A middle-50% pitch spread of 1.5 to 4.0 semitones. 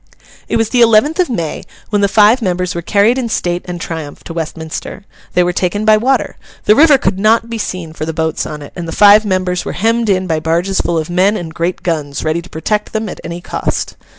No: average, 4.4 semitones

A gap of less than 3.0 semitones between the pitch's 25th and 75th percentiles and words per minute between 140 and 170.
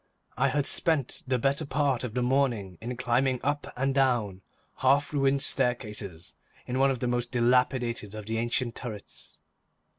Yes: narrow, 2.6 semitones; average, 160 wpm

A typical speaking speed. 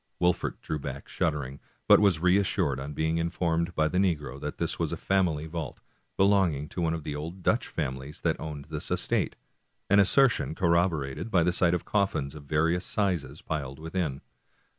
Yes: average, 180 wpm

